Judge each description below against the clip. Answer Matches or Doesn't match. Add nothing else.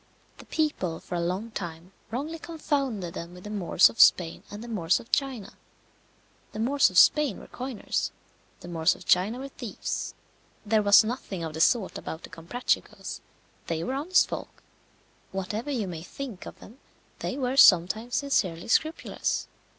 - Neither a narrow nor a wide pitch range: Doesn't match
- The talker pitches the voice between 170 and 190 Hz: Doesn't match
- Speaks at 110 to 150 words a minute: Doesn't match